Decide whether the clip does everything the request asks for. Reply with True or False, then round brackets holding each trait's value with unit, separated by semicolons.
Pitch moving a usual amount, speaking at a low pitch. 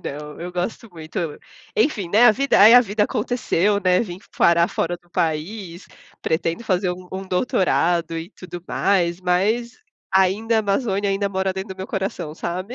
False (3.1 semitones; 190 Hz)